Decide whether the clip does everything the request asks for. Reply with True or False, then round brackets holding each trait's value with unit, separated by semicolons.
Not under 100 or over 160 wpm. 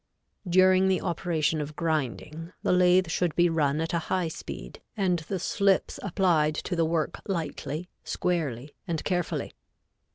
True (150 wpm)